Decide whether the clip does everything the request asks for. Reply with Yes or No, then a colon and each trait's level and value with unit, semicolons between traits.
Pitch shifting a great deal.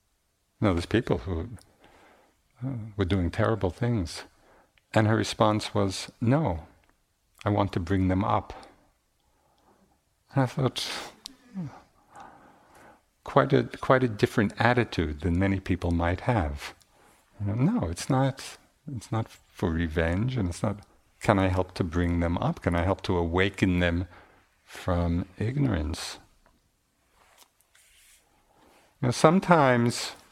No: average, 4.7 semitones